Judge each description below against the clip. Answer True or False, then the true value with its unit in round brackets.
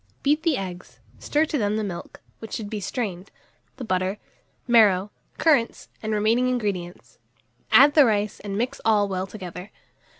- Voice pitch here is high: True (210 Hz)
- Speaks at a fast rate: False (160 wpm)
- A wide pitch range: False (4.3 semitones)